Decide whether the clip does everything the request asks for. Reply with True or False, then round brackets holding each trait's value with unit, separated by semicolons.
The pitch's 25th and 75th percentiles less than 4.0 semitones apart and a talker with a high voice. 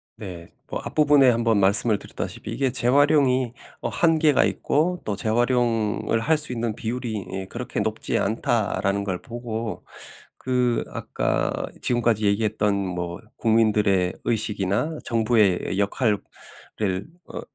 False (3.6 semitones; 115 Hz)